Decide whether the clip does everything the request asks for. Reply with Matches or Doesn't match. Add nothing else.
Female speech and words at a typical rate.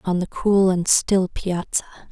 Matches